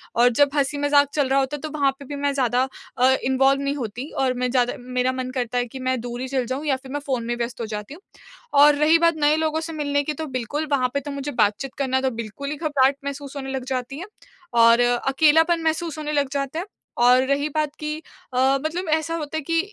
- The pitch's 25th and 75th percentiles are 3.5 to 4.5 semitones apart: No, average, 2.8 semitones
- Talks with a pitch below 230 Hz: No, very high, 275 Hz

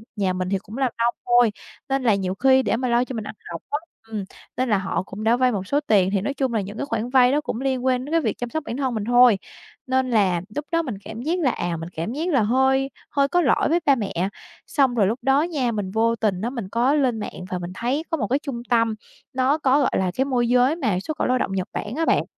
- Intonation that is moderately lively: Yes, average, 4.3 semitones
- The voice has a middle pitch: No, high, 245 Hz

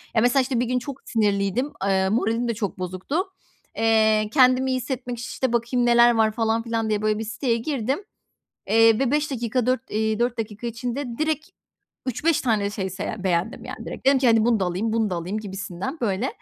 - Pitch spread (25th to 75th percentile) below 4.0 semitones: Yes, average, 2.9 semitones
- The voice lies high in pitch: Yes, high, 230 Hz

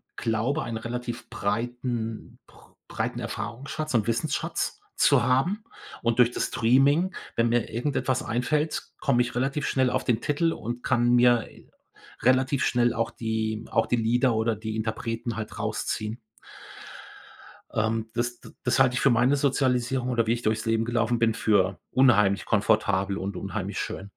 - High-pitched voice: No, low, 120 Hz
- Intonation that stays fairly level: Yes, narrow, 2.3 semitones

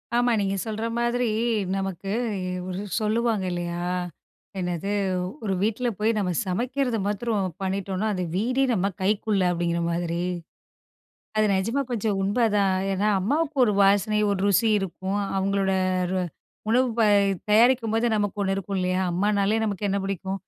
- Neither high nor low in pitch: No, high, 200 Hz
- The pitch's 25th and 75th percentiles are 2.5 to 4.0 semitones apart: Yes, average, 2.9 semitones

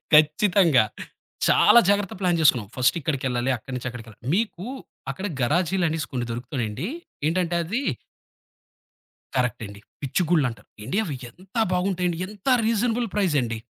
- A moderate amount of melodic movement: No, wide, 7.1 semitones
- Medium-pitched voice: Yes, medium, 160 Hz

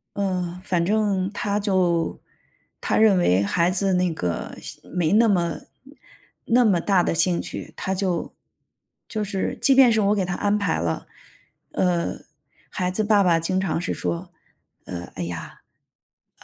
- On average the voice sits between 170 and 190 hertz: Yes, medium, 185 Hz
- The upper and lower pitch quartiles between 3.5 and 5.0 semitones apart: No, average, 3.1 semitones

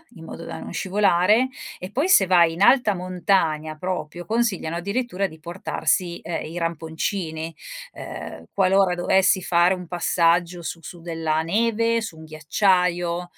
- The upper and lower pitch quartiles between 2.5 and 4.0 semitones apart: Yes, average, 2.9 semitones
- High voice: No, medium, 180 Hz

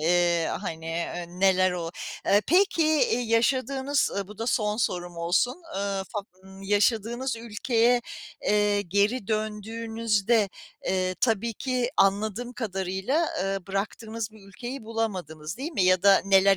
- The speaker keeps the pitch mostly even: No, average, 3.6 semitones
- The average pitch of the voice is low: No, high, 210 Hz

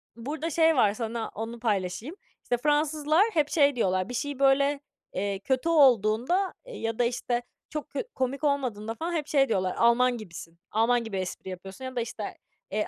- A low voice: No, high, 245 Hz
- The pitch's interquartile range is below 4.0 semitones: No, average, 5.1 semitones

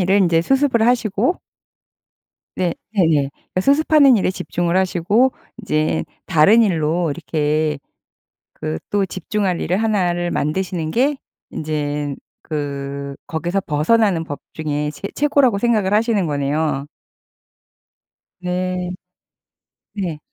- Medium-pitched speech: Yes, medium, 180 Hz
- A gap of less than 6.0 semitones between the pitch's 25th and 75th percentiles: Yes, wide, 5.5 semitones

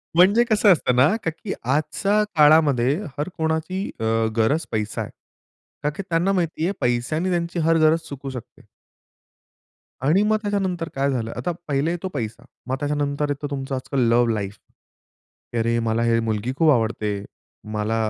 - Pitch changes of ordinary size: No, wide, 5.9 semitones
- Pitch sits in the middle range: Yes, medium, 145 Hz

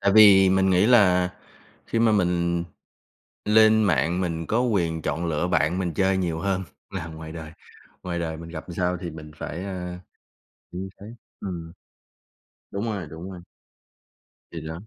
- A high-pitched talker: No, very low, 90 Hz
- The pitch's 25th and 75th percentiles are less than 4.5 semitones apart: Yes, average, 2.7 semitones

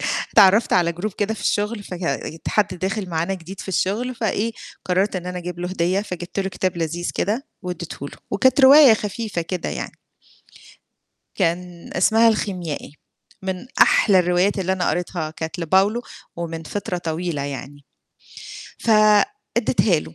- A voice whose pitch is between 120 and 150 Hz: No, medium, 185 Hz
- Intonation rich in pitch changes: No, average, 3.3 semitones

